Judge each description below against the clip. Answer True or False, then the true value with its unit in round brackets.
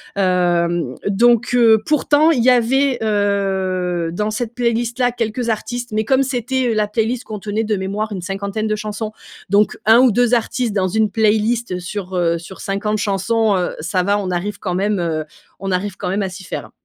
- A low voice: False (210 Hz)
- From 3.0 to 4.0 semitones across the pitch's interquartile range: True (3.6 semitones)